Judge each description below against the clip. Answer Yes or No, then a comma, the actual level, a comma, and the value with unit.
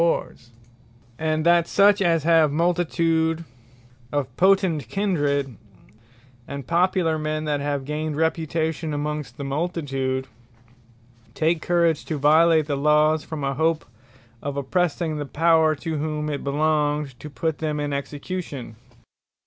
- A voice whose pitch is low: No, medium, 155 Hz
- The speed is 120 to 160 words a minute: Yes, slow, 135 wpm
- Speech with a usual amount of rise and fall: No, narrow, 2.3 semitones